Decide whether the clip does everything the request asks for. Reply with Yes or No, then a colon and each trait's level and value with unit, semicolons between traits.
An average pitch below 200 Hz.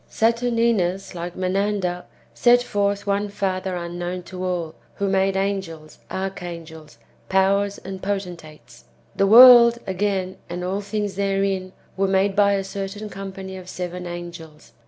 Yes: high, 190 Hz